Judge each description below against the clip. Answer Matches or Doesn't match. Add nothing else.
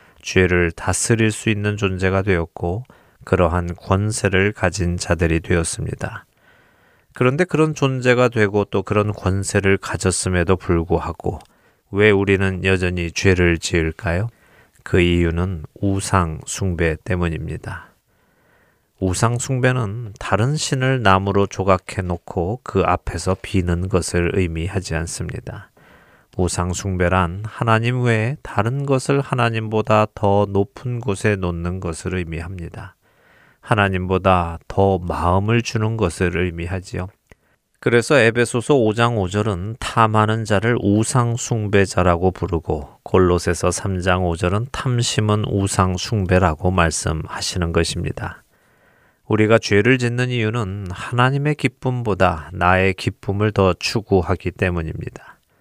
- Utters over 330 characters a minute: Doesn't match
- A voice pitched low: Matches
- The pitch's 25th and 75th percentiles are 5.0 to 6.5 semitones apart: Doesn't match